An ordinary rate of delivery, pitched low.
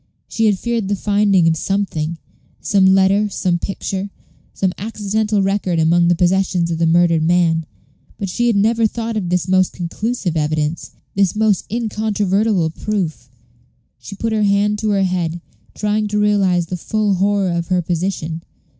No: average, 165 wpm; high, 195 Hz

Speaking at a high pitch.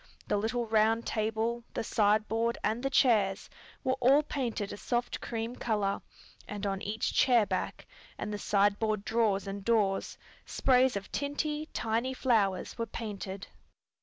Yes: high, 220 Hz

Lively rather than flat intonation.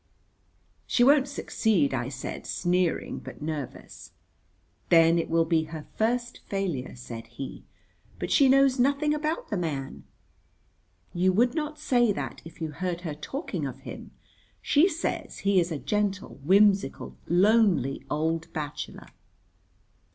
Yes: wide, 7.5 semitones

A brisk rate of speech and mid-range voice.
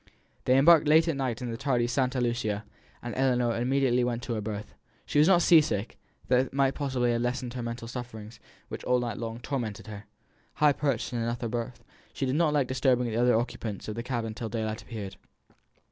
No: fast, 210 wpm; low, 120 Hz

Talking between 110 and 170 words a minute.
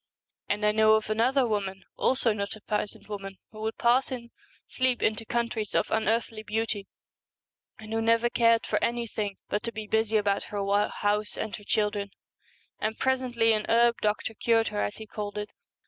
No: average, 185 wpm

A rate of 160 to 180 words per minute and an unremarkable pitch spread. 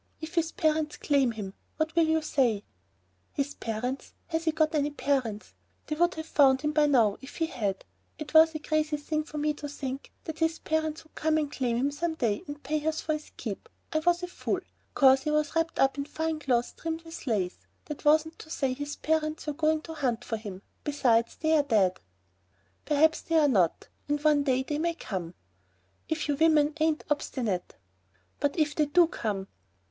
No: fast, 205 wpm; average, 3.2 semitones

